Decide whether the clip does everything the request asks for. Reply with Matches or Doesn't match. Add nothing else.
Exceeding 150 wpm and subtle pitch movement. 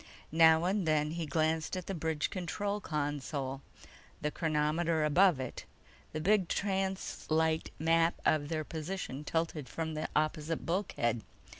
Doesn't match